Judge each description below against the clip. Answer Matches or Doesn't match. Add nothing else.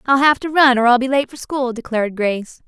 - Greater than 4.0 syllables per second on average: Matches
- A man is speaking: Doesn't match